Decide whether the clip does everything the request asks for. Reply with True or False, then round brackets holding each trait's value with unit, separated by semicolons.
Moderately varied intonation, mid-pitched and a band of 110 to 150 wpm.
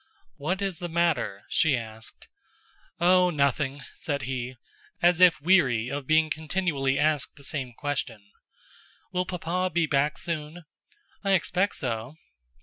True (4.6 semitones; 155 Hz; 135 wpm)